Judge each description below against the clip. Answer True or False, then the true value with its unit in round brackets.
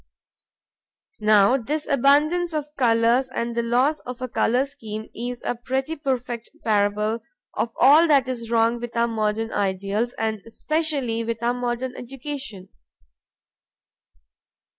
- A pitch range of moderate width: True (3.2 semitones)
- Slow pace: True (125 wpm)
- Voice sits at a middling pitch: False (240 Hz)